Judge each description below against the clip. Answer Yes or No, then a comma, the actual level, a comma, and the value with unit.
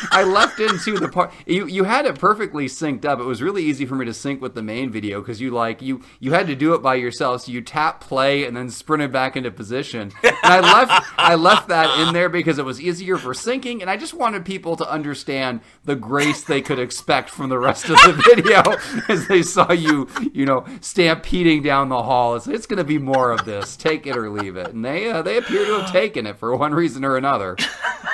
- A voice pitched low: No, medium, 145 Hz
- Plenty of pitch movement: Yes, wide, 5.7 semitones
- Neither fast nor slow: No, fast, 245 wpm